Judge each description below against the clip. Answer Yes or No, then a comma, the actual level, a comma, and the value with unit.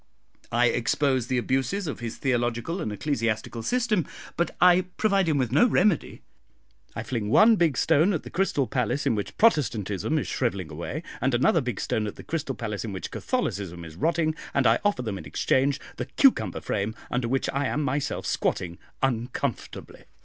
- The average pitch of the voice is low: Yes, low, 130 Hz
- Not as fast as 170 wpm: No, average, 180 wpm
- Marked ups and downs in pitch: Yes, wide, 6.3 semitones